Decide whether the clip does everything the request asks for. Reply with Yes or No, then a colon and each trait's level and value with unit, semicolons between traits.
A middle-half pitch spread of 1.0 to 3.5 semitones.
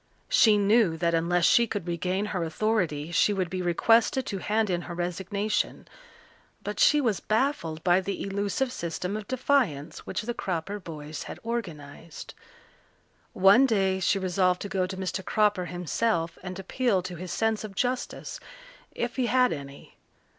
No: average, 4.0 semitones